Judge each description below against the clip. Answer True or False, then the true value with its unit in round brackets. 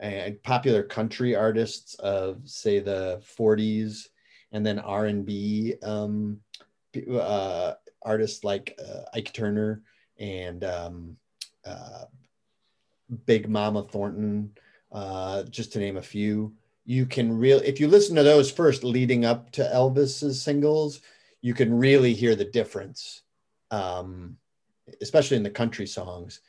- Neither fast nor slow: False (125 wpm)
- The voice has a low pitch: True (110 Hz)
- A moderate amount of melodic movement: True (3.7 semitones)